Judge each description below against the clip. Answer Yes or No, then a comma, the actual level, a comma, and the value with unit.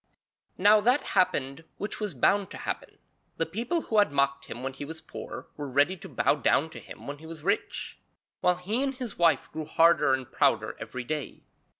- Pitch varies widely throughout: Yes, wide, 6.3 semitones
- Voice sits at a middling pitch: Yes, medium, 165 Hz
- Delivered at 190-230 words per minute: Yes, fast, 205 wpm